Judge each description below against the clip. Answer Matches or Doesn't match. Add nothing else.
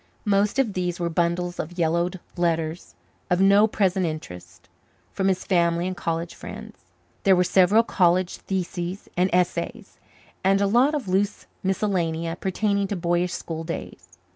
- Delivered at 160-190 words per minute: Doesn't match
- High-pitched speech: Doesn't match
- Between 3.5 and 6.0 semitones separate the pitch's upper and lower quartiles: Doesn't match